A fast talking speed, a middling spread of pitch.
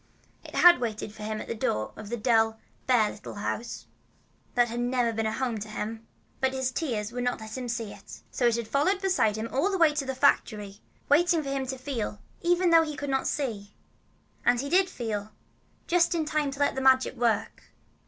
Yes: fast, 220 wpm; average, 4.6 semitones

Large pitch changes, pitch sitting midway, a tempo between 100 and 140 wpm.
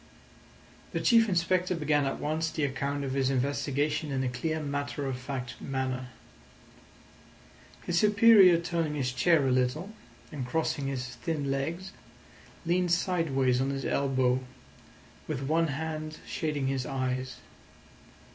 No: average, 3.7 semitones; medium, 145 Hz; slow, 135 wpm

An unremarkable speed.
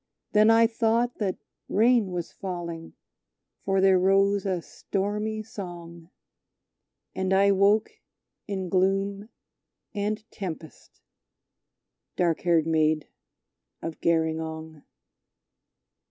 No: slow, 95 wpm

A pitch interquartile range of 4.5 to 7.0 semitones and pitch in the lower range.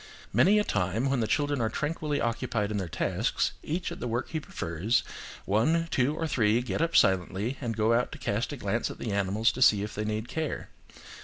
Yes: wide, 5.5 semitones; low, 115 Hz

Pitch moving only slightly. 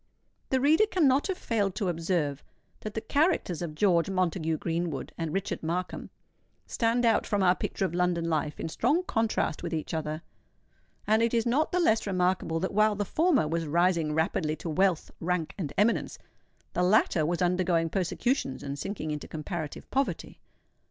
No: average, 5.2 semitones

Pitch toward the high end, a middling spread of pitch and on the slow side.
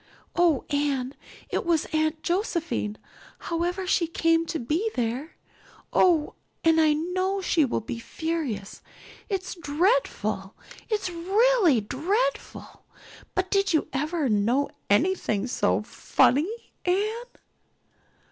Yes: very high, 330 Hz; average, 5.0 semitones; slow, 110 wpm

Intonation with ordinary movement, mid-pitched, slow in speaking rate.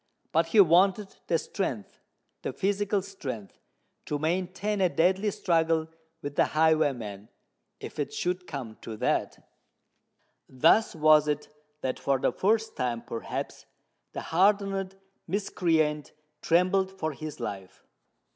Yes: average, 5.0 semitones; medium, 165 Hz; slow, 120 wpm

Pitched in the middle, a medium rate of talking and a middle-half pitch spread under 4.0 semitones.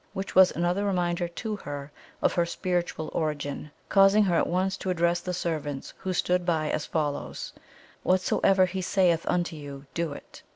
Yes: medium, 175 Hz; average, 170 wpm; average, 3.0 semitones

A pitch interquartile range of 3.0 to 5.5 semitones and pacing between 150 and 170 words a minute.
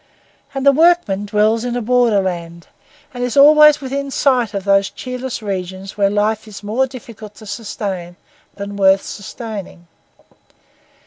No: average, 4.2 semitones; average, 140 wpm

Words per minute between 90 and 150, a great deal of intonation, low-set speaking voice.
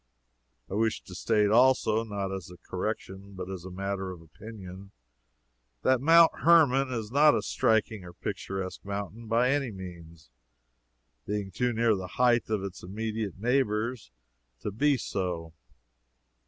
No: average, 140 wpm; average, 4.1 semitones; low, 105 Hz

